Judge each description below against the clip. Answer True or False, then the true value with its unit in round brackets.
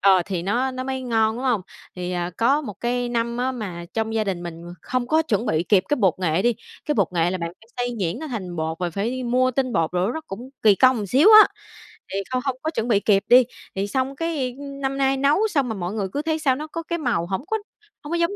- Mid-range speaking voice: False (240 Hz)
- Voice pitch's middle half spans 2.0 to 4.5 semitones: False (5.6 semitones)